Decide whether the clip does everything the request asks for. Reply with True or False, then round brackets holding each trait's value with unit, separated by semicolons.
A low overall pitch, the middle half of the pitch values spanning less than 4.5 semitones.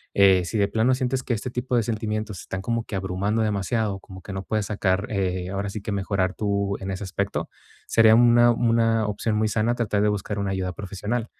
True (105 Hz; 2.7 semitones)